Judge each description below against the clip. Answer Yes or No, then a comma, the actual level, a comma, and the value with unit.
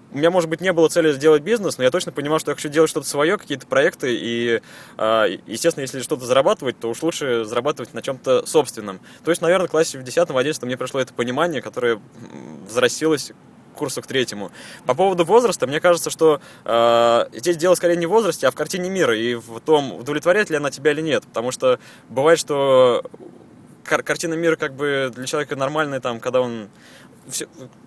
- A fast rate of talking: Yes, fast, 195 wpm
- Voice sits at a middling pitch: Yes, medium, 150 Hz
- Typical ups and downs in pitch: Yes, average, 4.6 semitones